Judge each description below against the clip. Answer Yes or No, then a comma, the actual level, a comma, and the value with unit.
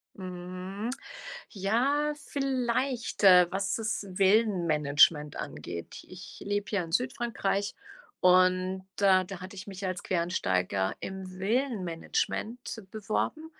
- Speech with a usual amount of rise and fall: Yes, average, 3.6 semitones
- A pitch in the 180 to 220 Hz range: Yes, high, 190 Hz